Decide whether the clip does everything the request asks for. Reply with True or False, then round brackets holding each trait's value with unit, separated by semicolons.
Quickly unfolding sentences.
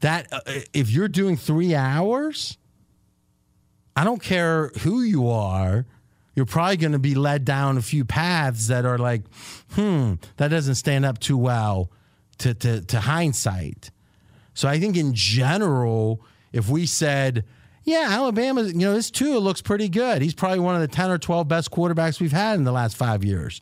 False (185 wpm)